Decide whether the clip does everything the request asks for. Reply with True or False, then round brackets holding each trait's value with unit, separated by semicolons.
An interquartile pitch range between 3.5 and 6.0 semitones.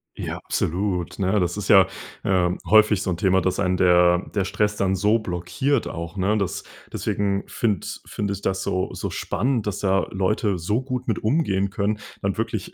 False (2.4 semitones)